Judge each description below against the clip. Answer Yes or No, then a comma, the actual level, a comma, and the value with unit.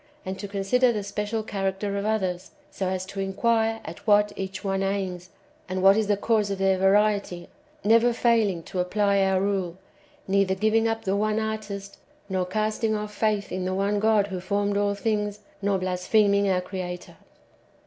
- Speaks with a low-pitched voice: No, high, 200 Hz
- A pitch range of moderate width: No, narrow, 1.9 semitones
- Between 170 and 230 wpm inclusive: Yes, average, 180 wpm